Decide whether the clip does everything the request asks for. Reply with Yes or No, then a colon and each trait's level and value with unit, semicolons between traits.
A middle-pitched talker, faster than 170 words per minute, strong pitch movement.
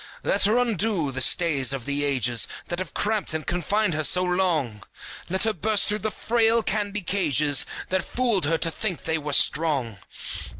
Yes: medium, 175 Hz; average, 180 wpm; wide, 6.4 semitones